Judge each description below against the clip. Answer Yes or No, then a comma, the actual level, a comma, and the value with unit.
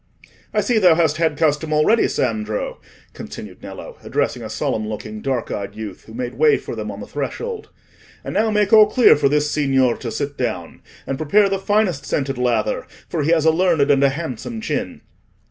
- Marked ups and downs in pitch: Yes, wide, 6.8 semitones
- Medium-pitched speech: Yes, medium, 150 Hz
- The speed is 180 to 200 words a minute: Yes, average, 195 wpm